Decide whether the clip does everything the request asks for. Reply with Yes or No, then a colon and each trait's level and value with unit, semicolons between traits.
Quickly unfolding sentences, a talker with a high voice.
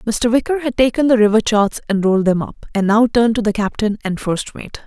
Yes: fast, 245 wpm; high, 220 Hz